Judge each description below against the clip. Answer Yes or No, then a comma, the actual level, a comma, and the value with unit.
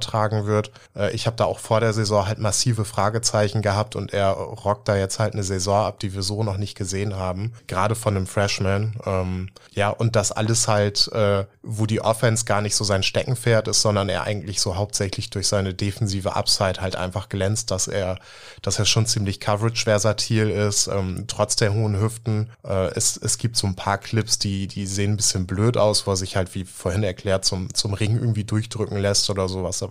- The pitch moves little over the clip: Yes, narrow, 1.9 semitones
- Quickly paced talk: Yes, fast, 215 wpm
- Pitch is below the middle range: Yes, low, 105 Hz